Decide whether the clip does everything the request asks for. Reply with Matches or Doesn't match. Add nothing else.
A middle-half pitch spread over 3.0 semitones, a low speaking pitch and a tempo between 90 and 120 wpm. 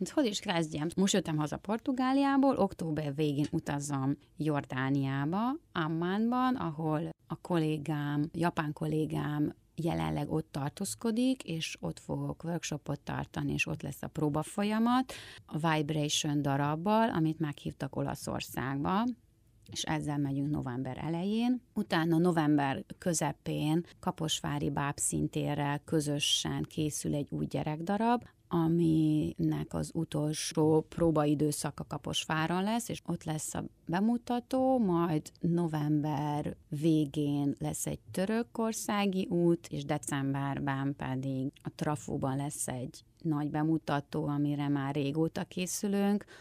Doesn't match